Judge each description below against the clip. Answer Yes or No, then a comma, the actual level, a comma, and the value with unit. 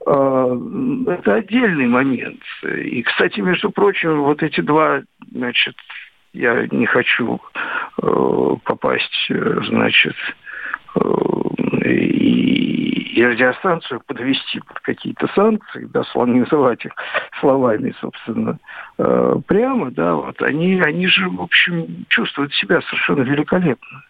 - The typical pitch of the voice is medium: Yes, medium, 180 Hz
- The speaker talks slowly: Yes, slow, 95 wpm